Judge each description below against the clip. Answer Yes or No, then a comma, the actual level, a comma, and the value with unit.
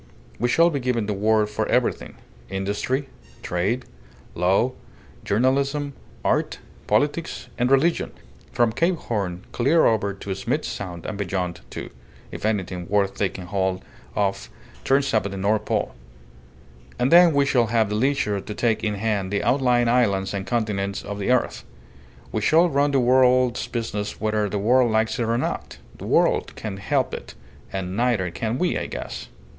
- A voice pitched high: No, low, 110 Hz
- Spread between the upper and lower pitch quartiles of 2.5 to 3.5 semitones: No, average, 4.3 semitones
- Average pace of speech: Yes, average, 165 wpm